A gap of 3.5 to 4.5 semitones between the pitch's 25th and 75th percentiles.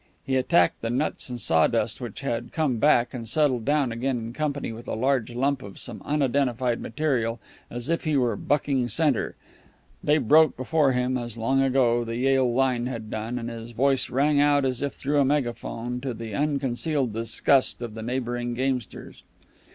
No: average, 2.9 semitones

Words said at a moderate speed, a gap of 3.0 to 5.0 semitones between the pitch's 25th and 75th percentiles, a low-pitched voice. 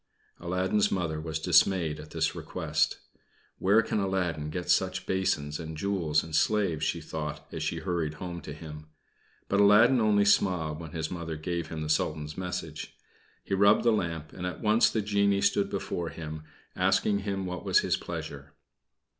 Yes: average, 170 wpm; average, 4.0 semitones; very low, 85 Hz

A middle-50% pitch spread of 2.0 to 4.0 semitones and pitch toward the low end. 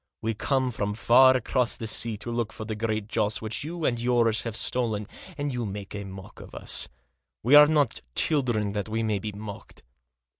Yes: average, 2.9 semitones; low, 115 Hz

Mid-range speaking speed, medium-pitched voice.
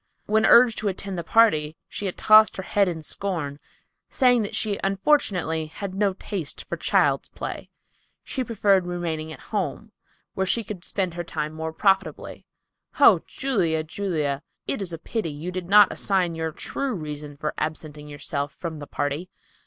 Yes: average, 170 wpm; medium, 180 Hz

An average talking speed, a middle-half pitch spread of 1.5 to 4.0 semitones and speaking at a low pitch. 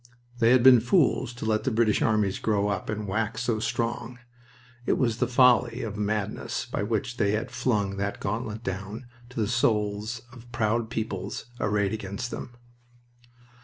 Yes: average, 170 wpm; narrow, 2.5 semitones; low, 110 Hz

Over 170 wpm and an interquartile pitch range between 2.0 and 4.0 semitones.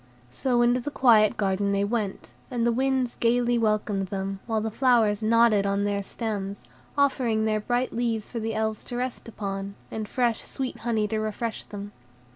Yes: average, 180 wpm; average, 2.8 semitones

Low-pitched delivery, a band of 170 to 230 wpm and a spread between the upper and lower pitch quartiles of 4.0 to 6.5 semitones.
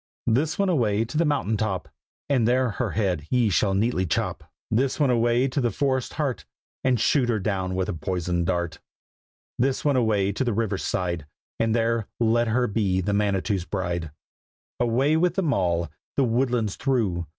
Yes: low, 115 Hz; average, 180 wpm; average, 5.2 semitones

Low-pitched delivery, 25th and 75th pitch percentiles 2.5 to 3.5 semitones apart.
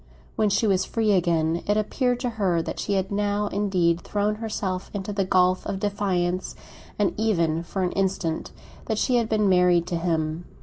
No: high, 195 Hz; average, 2.9 semitones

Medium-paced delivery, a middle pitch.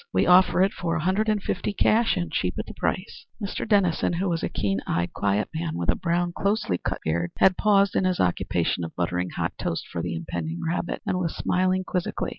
No: fast, 225 wpm; medium, 175 Hz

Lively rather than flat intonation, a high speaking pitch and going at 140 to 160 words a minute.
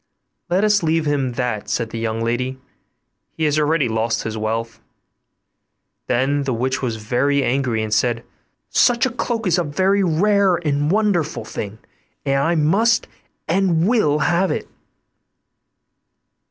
No: wide, 7.1 semitones; medium, 145 Hz; average, 145 wpm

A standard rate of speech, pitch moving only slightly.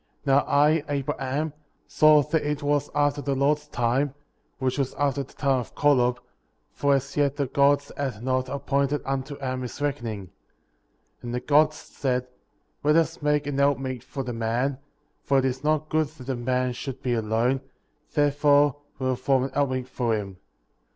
Yes: average, 185 wpm; narrow, 2.2 semitones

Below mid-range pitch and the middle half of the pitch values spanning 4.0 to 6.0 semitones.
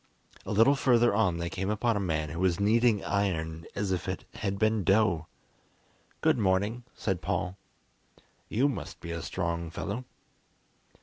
Yes: low, 100 Hz; average, 4.4 semitones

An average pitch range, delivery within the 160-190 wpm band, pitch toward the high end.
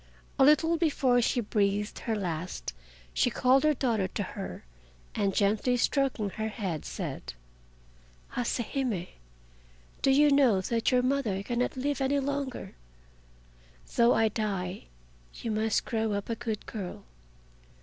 No: average, 4.7 semitones; average, 140 wpm; high, 230 Hz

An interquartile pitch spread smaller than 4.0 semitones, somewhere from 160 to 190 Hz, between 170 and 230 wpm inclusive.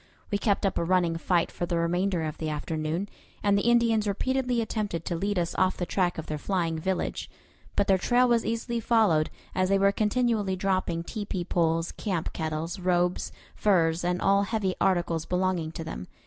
Yes: average, 3.4 semitones; medium, 185 Hz; average, 190 wpm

